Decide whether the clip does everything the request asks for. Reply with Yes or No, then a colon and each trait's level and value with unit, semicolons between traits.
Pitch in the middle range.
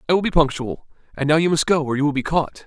Yes: medium, 150 Hz